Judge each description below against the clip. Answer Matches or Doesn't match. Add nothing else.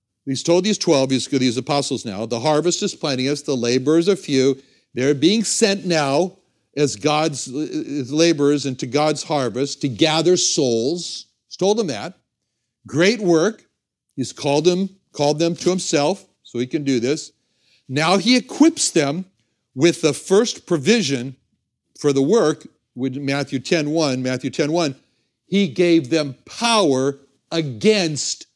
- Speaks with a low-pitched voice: Doesn't match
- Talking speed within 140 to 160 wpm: Matches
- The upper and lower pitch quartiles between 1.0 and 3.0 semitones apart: Doesn't match